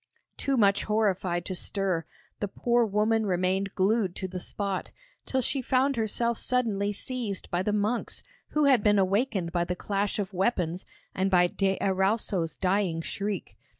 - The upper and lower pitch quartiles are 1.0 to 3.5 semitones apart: Yes, average, 3.1 semitones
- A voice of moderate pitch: No, high, 200 Hz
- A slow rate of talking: No, average, 160 wpm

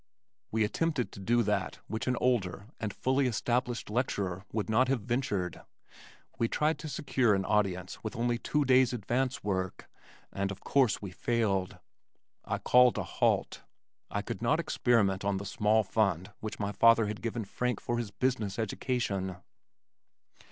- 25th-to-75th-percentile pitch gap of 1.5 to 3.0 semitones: No, average, 3.9 semitones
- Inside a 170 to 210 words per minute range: No, average, 160 wpm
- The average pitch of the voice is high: No, low, 110 Hz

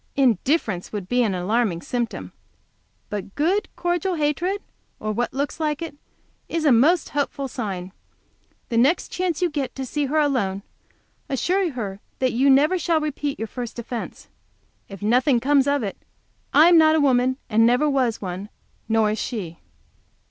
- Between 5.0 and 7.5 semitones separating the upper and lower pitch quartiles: Yes, wide, 5.4 semitones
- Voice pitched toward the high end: Yes, very high, 260 Hz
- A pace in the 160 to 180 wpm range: Yes, average, 165 wpm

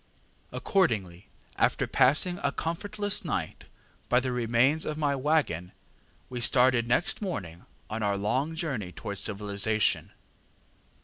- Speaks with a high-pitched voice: No, low, 125 Hz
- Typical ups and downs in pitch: No, wide, 7.1 semitones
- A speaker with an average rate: No, slow, 120 wpm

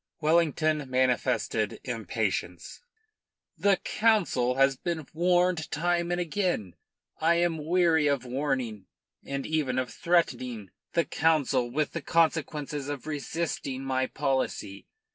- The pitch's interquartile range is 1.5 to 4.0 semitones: No, average, 4.5 semitones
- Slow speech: Yes, slow, 115 wpm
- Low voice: No, medium, 150 Hz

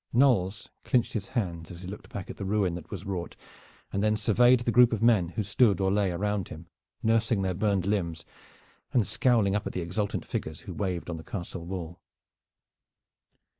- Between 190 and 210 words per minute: Yes, average, 195 wpm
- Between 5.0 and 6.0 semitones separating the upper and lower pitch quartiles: No, average, 3.6 semitones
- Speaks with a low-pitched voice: Yes, low, 100 Hz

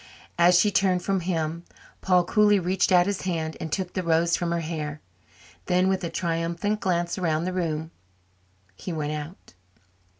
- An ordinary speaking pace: Yes, average, 170 wpm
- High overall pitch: No, medium, 175 Hz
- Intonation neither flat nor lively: No, narrow, 2.2 semitones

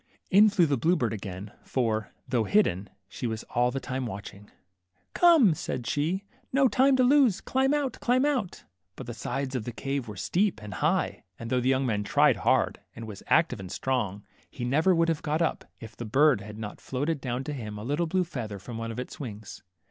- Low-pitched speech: Yes, low, 130 Hz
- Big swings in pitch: Yes, wide, 7.5 semitones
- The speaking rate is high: Yes, fast, 220 wpm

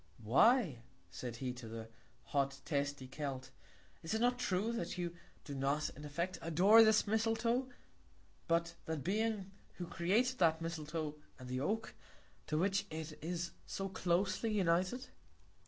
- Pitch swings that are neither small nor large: No, wide, 6.1 semitones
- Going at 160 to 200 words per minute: No, average, 145 wpm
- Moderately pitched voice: Yes, medium, 170 Hz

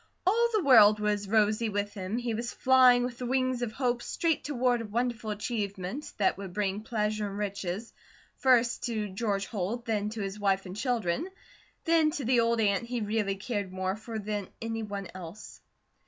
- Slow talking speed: No, average, 185 wpm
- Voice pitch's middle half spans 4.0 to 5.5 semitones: No, average, 3.3 semitones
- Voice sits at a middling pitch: No, high, 215 Hz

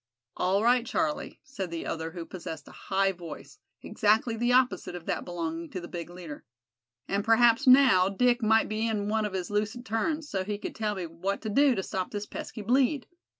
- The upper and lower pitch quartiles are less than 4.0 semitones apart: No, average, 4.8 semitones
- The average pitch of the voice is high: Yes, high, 210 Hz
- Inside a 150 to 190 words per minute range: No, fast, 205 wpm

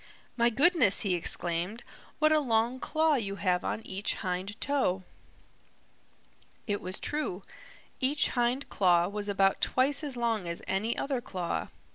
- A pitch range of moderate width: No, wide, 5.7 semitones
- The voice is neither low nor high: No, high, 220 Hz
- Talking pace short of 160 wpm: Yes, average, 145 wpm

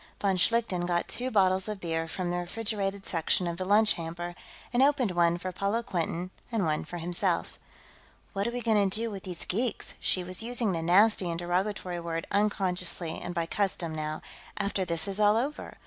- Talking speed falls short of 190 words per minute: No, average, 195 wpm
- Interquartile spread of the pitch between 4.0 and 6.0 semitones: No, average, 3.3 semitones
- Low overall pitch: No, medium, 185 Hz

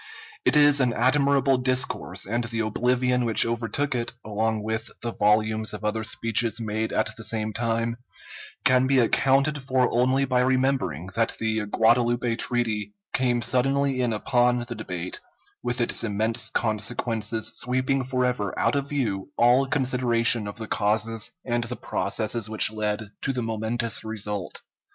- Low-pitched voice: Yes, low, 115 Hz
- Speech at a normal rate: Yes, average, 150 wpm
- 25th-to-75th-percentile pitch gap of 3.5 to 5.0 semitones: No, narrow, 2.6 semitones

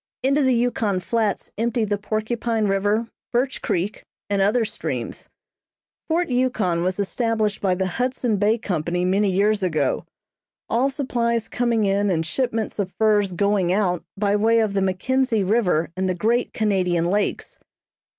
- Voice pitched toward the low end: No, high, 210 Hz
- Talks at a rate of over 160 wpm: No, average, 150 wpm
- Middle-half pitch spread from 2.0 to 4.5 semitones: Yes, average, 3.6 semitones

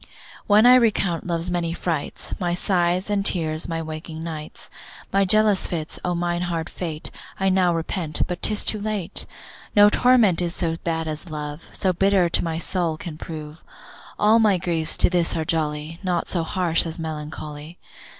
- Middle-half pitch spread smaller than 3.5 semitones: Yes, average, 2.9 semitones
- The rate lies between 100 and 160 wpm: No, average, 175 wpm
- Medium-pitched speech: Yes, medium, 170 Hz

